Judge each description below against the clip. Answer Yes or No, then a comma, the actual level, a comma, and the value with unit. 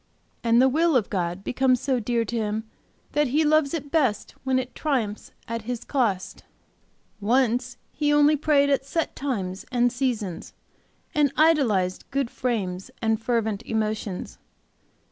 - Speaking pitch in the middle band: No, high, 245 Hz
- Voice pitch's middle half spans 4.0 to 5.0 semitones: Yes, average, 4.4 semitones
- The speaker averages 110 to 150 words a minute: Yes, average, 145 wpm